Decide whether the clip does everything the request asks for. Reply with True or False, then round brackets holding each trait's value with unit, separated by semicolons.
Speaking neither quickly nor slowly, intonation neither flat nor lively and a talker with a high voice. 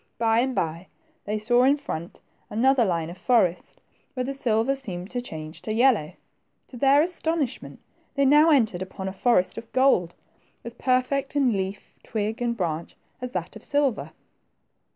False (165 wpm; 6.0 semitones; 235 Hz)